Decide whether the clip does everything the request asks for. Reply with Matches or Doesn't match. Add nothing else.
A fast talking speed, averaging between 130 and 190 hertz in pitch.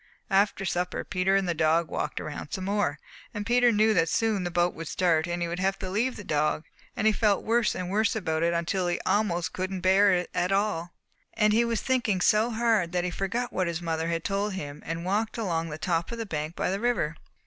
Matches